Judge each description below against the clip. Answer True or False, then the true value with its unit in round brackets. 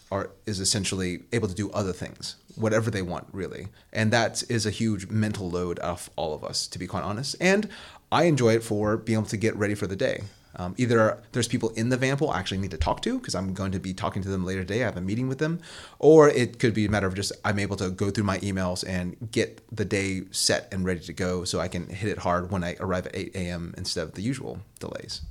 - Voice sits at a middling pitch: False (100 Hz)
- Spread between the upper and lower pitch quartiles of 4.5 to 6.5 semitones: False (3.4 semitones)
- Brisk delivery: True (260 wpm)